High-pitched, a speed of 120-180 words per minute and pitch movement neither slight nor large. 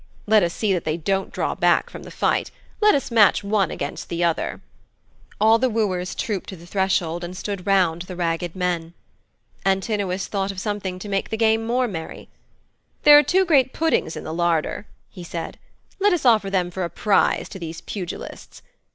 No: high, 195 Hz; average, 195 wpm; average, 3.9 semitones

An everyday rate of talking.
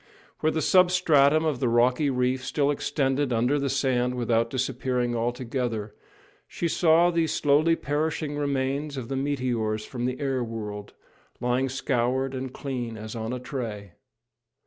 Yes: average, 145 wpm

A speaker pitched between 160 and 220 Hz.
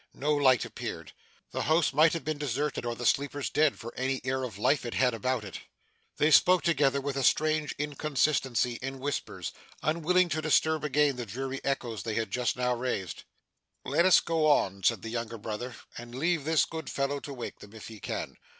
No: low, 135 Hz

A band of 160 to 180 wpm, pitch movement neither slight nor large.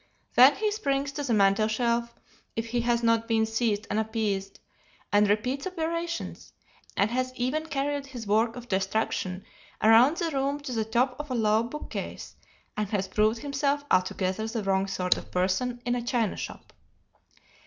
Yes: average, 170 wpm; average, 4.4 semitones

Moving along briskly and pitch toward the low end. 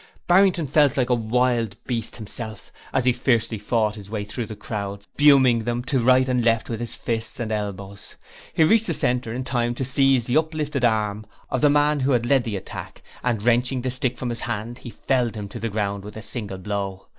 Yes: fast, 215 wpm; low, 120 Hz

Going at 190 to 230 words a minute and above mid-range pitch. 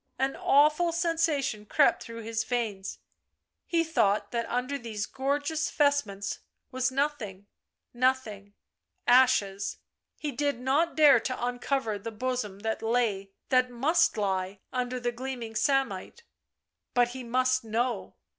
No: slow, 135 wpm; very high, 250 Hz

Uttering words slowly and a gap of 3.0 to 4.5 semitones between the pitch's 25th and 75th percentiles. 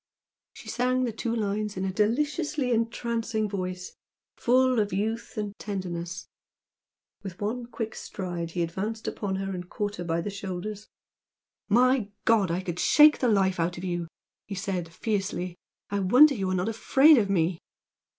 No: average, 165 wpm; average, 3.9 semitones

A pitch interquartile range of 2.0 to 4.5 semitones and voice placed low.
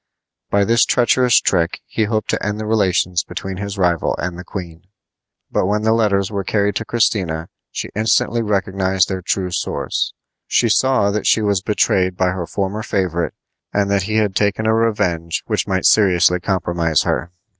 Yes: average, 2.8 semitones; low, 100 Hz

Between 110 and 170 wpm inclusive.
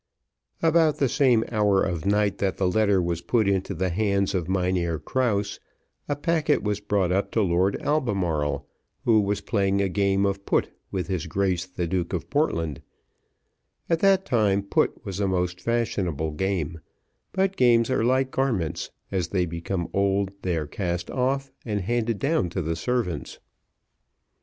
Yes: average, 165 wpm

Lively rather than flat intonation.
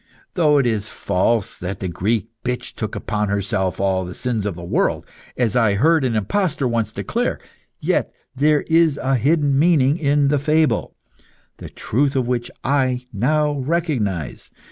Yes: wide, 5.9 semitones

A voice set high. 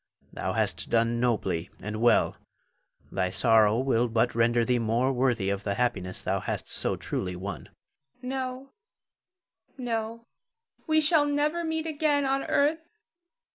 No: low, 125 Hz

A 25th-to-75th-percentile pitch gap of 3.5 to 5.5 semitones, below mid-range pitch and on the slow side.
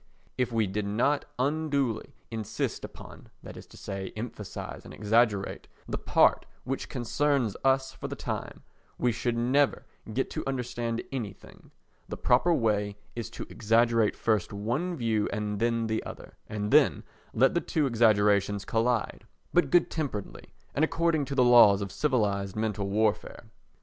No: average, 4.1 semitones; low, 115 Hz; average, 150 wpm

